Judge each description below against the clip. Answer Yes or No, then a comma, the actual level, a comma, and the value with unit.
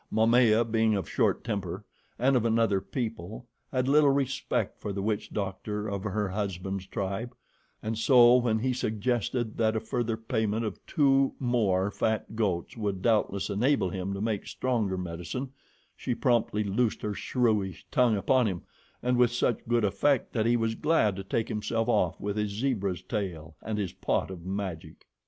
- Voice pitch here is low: Yes, low, 110 Hz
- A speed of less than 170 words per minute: No, average, 175 wpm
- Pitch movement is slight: No, average, 3.5 semitones